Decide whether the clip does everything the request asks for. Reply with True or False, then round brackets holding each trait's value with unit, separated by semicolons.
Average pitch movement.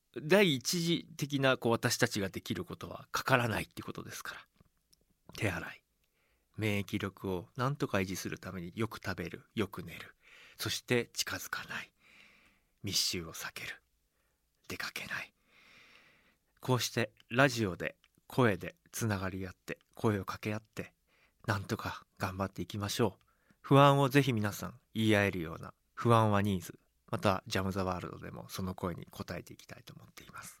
True (4.5 semitones)